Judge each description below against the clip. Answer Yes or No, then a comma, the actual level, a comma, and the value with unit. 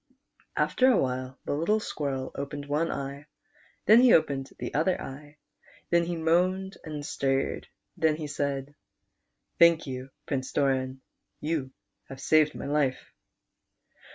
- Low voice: No, medium, 145 Hz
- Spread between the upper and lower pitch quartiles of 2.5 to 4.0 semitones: Yes, average, 3.4 semitones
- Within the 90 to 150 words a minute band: Yes, slow, 135 wpm